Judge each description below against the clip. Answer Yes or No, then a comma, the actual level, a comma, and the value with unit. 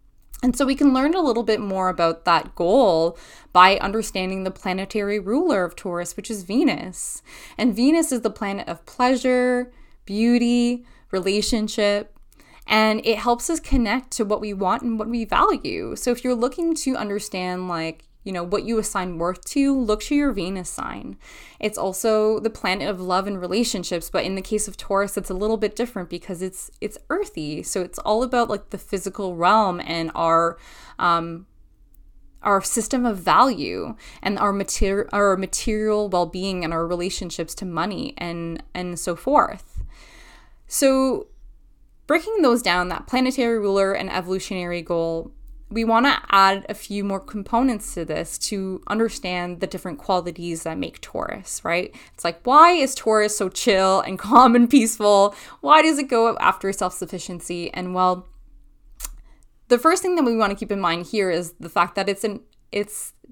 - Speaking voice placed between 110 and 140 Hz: No, high, 205 Hz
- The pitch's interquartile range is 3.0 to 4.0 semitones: No, average, 4.8 semitones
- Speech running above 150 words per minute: Yes, average, 175 wpm